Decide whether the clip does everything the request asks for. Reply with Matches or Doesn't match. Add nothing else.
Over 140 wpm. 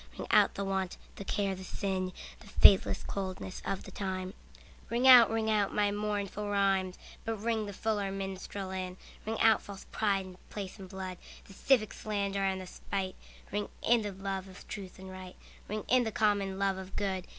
Matches